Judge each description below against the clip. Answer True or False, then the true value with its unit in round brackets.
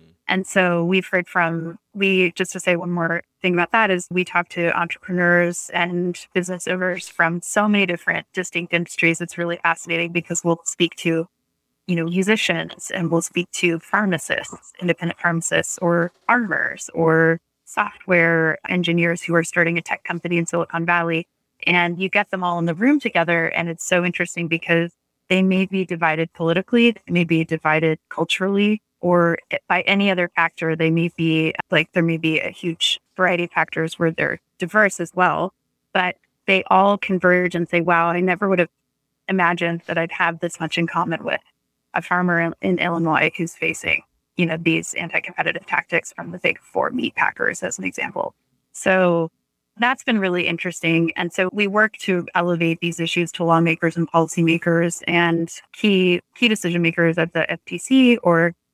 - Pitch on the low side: False (175 Hz)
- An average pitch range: False (1.6 semitones)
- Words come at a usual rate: True (175 wpm)